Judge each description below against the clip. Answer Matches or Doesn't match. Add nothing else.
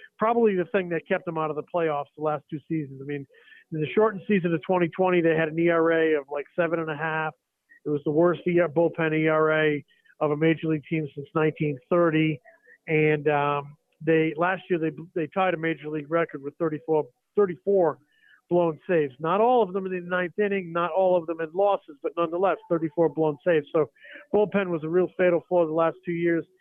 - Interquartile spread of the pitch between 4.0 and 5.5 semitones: Doesn't match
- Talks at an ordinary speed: Doesn't match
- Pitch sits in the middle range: Matches